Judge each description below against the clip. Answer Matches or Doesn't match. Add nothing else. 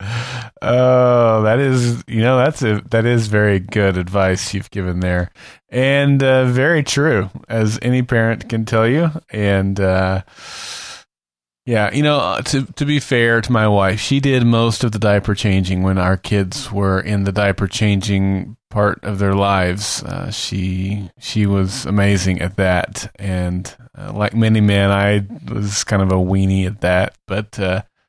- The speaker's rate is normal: Matches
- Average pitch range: Matches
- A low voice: Matches